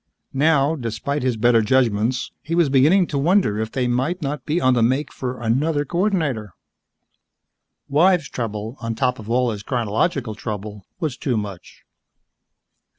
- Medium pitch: No, low, 125 Hz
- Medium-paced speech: Yes, average, 150 wpm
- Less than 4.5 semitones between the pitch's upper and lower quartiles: No, average, 4.9 semitones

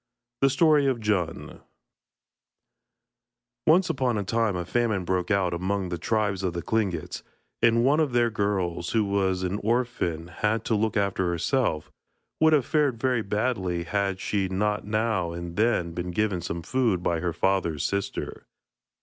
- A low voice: Yes, low, 100 Hz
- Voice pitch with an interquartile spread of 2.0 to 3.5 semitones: No, average, 4.7 semitones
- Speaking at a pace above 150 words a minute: Yes, average, 165 wpm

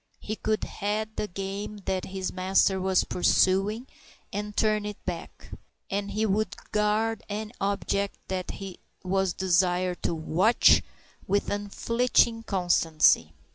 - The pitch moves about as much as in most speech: No, narrow, 2.2 semitones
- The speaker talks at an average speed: No, slow, 125 wpm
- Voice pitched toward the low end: No, high, 200 Hz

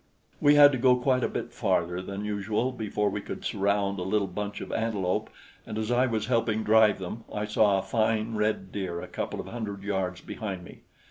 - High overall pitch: No, low, 105 Hz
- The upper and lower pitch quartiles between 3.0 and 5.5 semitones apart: No, narrow, 2.4 semitones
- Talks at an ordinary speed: No, fast, 210 wpm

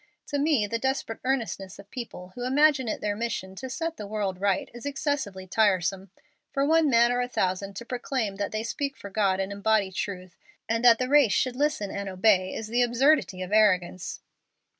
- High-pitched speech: Yes, high, 220 Hz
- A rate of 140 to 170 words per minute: No, average, 200 wpm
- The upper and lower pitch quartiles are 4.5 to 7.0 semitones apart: Yes, average, 4.8 semitones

